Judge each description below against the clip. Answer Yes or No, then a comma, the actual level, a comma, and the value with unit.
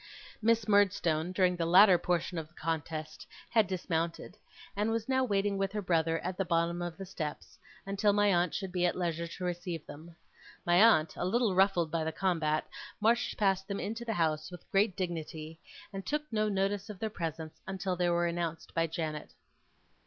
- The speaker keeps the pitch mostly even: No, average, 3.3 semitones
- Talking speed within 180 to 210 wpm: Yes, average, 190 wpm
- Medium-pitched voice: Yes, medium, 180 Hz